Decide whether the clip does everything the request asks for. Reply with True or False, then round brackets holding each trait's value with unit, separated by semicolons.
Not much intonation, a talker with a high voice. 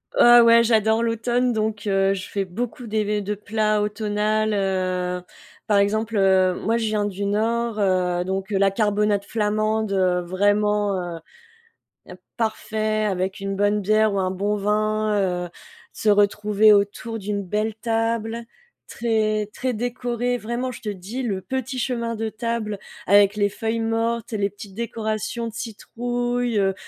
True (2.2 semitones; 215 Hz)